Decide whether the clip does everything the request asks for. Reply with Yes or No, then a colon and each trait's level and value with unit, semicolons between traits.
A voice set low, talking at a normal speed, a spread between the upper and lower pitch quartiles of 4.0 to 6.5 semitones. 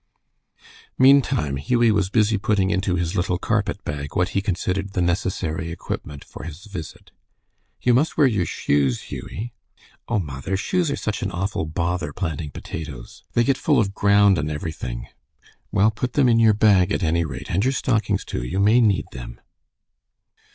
Yes: very low, 95 Hz; average, 170 wpm; average, 5.1 semitones